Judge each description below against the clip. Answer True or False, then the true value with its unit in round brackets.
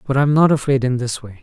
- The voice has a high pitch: False (130 Hz)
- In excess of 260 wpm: True (295 wpm)